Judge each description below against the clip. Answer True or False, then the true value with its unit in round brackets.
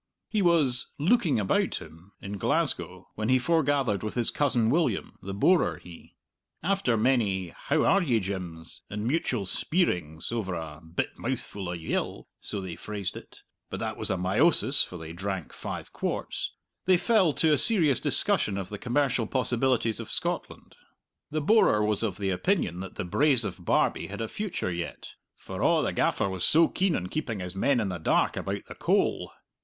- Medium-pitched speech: False (110 Hz)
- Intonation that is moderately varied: False (7.6 semitones)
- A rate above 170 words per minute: True (180 wpm)